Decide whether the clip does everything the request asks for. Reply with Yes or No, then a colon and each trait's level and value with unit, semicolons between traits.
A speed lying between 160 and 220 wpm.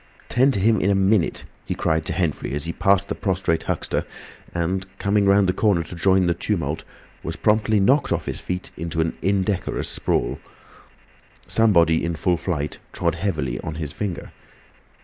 Yes: average, 175 wpm